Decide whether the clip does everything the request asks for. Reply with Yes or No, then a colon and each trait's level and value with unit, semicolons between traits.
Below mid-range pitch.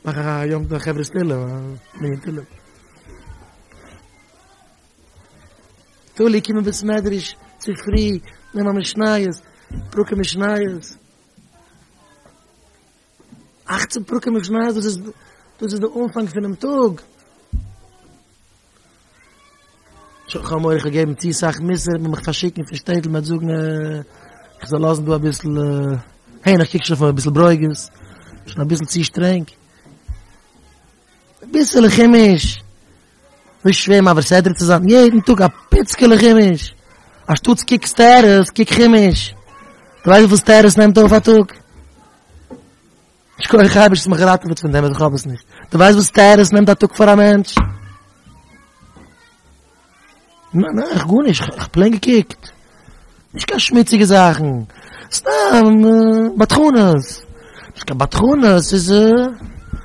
No: medium, 180 Hz